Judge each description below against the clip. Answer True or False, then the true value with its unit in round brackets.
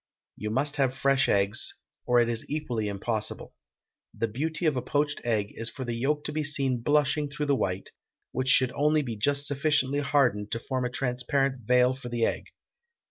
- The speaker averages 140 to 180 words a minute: False (190 wpm)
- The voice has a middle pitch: False (130 Hz)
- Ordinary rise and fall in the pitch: True (3.6 semitones)